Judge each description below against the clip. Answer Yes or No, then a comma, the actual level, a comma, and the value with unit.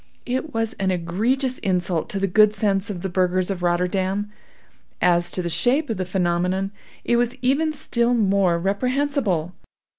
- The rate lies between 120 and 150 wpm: No, average, 160 wpm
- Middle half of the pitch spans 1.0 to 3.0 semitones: No, average, 4.8 semitones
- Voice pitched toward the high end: Yes, high, 195 Hz